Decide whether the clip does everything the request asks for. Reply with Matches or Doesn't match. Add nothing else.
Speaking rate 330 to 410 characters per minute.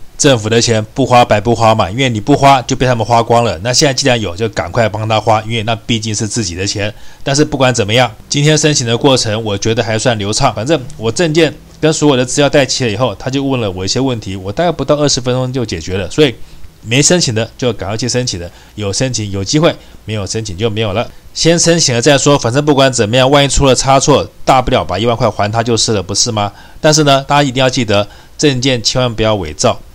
Matches